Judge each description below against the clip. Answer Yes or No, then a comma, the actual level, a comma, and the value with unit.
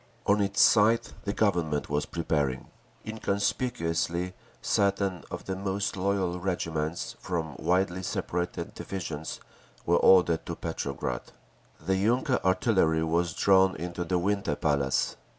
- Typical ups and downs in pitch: Yes, average, 3.2 semitones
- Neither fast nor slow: No, slow, 120 wpm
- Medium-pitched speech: No, very low, 90 Hz